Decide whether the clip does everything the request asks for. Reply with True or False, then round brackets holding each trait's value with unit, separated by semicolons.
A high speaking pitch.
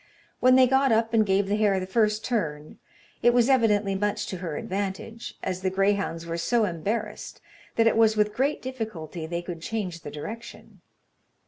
True (205 Hz)